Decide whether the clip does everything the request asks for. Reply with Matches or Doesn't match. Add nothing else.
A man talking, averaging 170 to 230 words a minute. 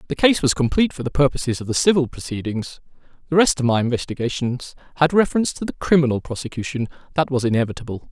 Matches